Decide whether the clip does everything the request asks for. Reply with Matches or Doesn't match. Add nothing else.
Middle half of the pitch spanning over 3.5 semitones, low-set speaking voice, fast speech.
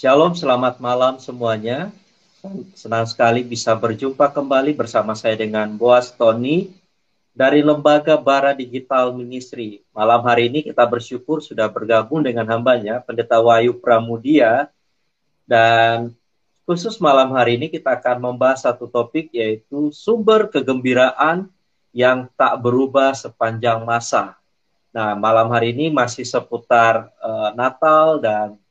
Doesn't match